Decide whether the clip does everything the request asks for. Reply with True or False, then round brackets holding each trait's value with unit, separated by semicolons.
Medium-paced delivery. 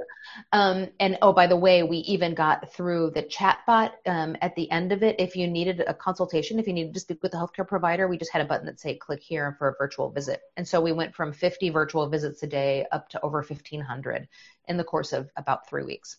False (250 wpm)